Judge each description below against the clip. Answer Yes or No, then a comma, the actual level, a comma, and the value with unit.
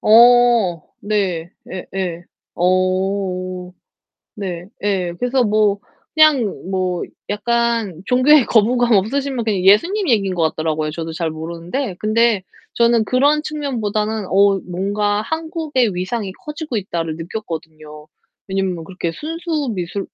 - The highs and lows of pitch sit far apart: No, average, 5.0 semitones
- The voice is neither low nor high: No, high, 205 Hz